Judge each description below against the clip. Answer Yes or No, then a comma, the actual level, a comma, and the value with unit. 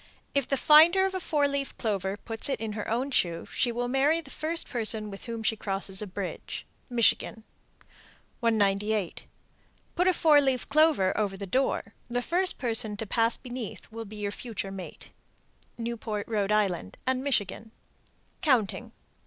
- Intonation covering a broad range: No, average, 4.9 semitones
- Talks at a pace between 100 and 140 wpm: No, average, 160 wpm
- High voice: Yes, high, 230 Hz